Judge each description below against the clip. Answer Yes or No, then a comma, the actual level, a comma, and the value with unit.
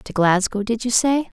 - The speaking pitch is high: Yes, high, 225 Hz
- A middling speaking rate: No, fast, 215 wpm